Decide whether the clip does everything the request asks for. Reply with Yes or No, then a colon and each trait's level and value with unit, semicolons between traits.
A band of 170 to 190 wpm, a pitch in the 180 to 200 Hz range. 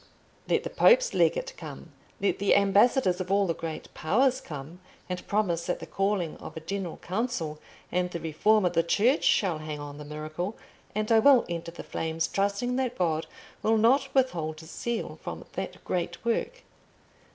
Yes: average, 180 wpm; high, 190 Hz